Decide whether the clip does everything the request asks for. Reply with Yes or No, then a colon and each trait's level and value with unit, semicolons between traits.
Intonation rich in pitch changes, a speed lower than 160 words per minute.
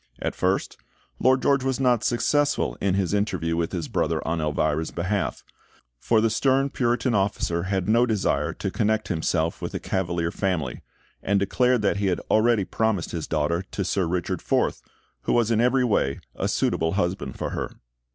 No: wide, 5.7 semitones; average, 180 wpm